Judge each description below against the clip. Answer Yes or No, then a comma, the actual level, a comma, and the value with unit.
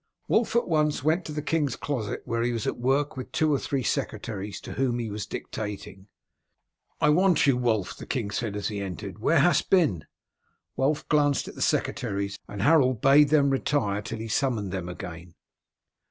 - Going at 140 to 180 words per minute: No, average, 190 wpm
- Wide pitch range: Yes, wide, 6.1 semitones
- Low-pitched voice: Yes, low, 120 Hz